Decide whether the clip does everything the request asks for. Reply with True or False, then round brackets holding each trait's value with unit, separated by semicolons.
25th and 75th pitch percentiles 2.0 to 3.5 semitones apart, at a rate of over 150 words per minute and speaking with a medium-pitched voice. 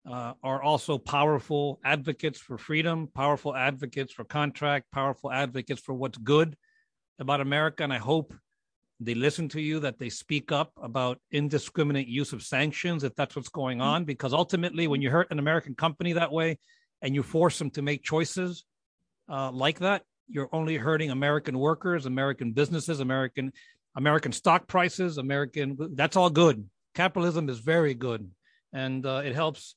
True (3.1 semitones; 175 wpm; 145 Hz)